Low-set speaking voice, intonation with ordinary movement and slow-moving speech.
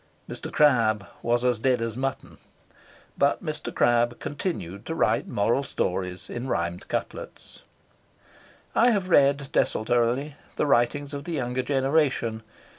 Yes: low, 125 Hz; average, 3.6 semitones; slow, 130 wpm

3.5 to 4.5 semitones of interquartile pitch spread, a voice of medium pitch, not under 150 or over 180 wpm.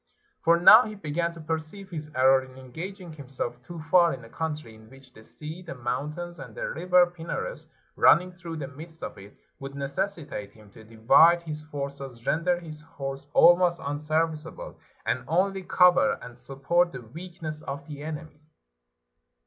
Yes: average, 4.2 semitones; medium, 155 Hz; average, 170 wpm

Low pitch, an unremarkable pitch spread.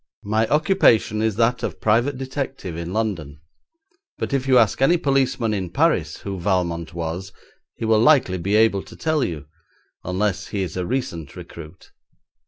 No: low, 105 Hz; wide, 6.6 semitones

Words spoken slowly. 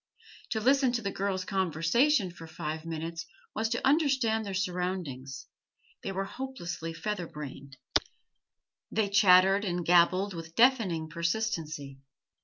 Yes: slow, 125 wpm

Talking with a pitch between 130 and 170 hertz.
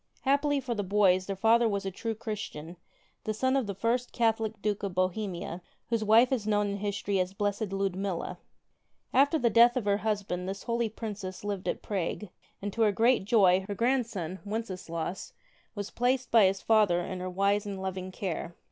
No: high, 205 Hz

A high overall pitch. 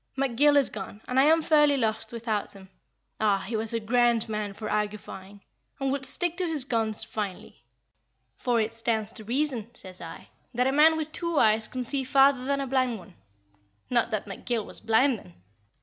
Yes: high, 235 Hz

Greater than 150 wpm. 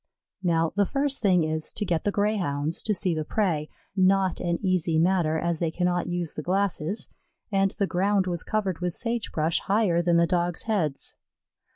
Yes: average, 185 wpm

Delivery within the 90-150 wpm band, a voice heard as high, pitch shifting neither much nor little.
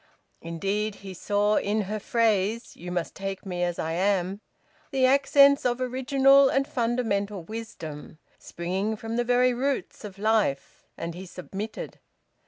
Yes: average, 145 wpm; high, 210 Hz; average, 4.6 semitones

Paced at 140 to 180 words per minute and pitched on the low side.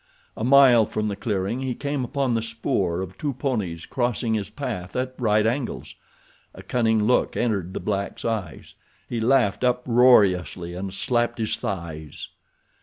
Yes: average, 155 wpm; low, 115 Hz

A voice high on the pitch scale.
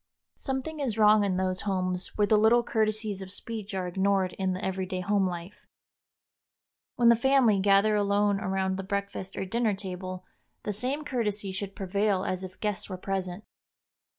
Yes: high, 200 Hz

